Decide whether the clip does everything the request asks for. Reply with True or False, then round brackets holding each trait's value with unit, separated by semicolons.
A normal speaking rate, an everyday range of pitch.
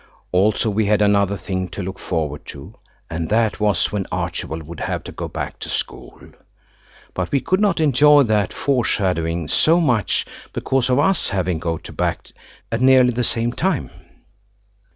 False (170 wpm; 6.1 semitones)